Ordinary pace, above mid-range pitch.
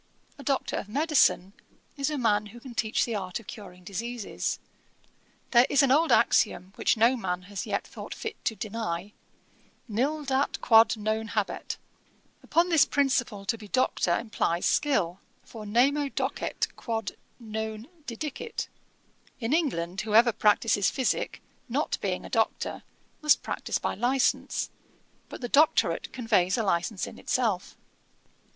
Yes: average, 145 wpm; high, 225 Hz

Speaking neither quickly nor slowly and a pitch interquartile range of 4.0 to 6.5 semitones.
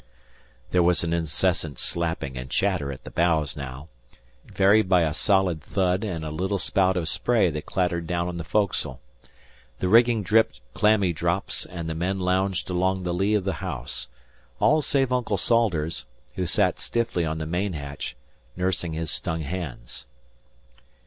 No: average, 165 wpm; average, 3.2 semitones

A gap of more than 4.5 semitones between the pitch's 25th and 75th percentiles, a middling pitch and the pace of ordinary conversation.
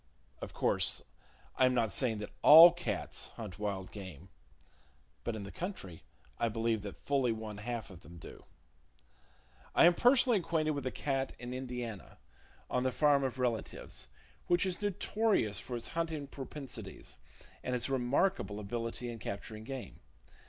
No: wide, 5.4 semitones; low, 125 Hz; average, 155 wpm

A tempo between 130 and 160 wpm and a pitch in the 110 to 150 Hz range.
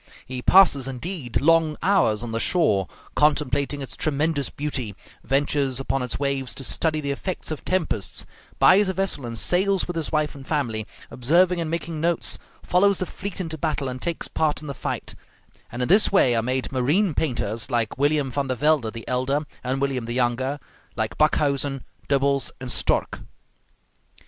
No: average, 175 wpm; medium, 140 Hz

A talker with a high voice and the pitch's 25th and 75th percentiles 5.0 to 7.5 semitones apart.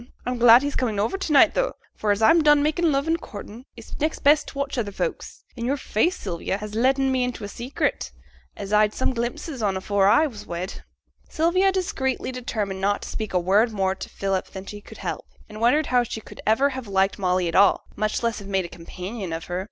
Yes: high, 225 Hz; wide, 5.4 semitones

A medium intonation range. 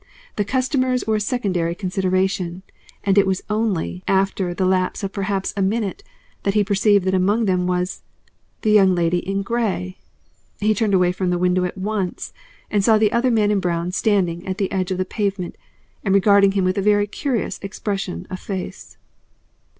No: narrow, 2.2 semitones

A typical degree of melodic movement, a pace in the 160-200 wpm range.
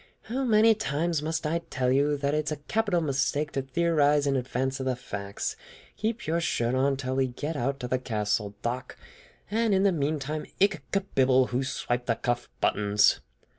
Yes: average, 4.5 semitones; average, 190 wpm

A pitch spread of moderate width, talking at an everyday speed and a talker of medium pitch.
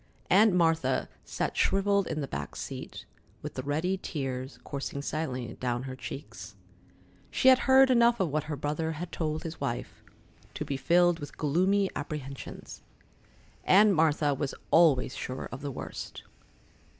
Yes: average, 4.8 semitones; average, 150 wpm; medium, 155 Hz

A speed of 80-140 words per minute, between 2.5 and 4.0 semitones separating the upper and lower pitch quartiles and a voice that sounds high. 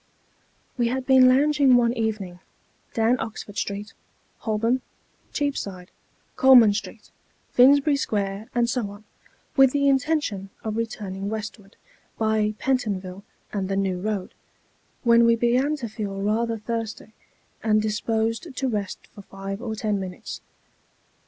Yes: slow, 135 wpm; average, 3.5 semitones; high, 220 Hz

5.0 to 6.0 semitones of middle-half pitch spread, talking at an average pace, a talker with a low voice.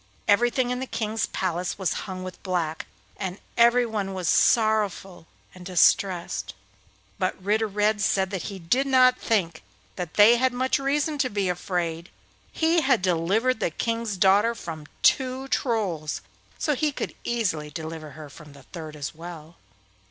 No: wide, 5.6 semitones; average, 150 wpm; high, 195 Hz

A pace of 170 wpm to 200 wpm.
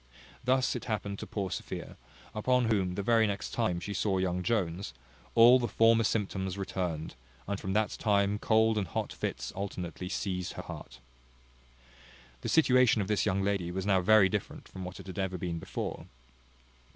Yes: average, 175 wpm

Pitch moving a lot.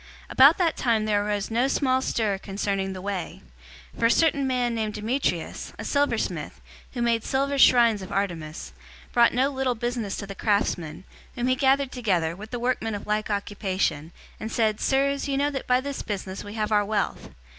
No: average, 4.4 semitones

